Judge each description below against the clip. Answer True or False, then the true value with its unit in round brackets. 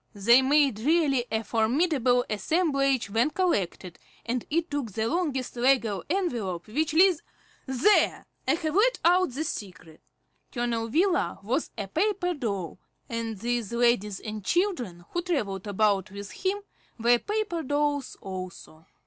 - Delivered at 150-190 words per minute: False (140 wpm)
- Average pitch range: False (7.1 semitones)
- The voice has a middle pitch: False (245 Hz)